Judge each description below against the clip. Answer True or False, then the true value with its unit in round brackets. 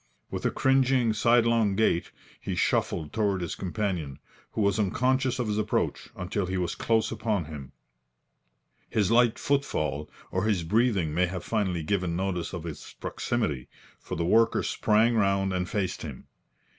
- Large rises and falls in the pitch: False (4.4 semitones)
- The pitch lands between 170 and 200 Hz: False (100 Hz)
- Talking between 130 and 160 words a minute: True (155 wpm)